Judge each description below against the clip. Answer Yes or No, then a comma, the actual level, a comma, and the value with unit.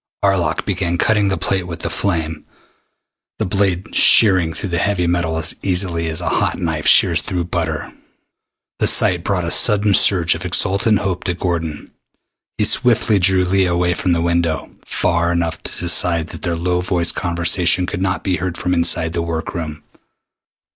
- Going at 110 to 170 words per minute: No, average, 180 wpm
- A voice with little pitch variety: Yes, narrow, 1.9 semitones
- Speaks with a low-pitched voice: Yes, very low, 90 Hz